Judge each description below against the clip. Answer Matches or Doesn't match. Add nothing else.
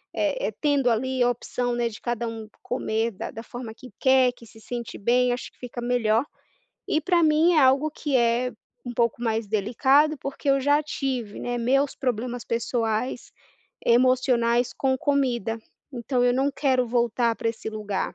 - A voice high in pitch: Matches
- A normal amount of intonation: Doesn't match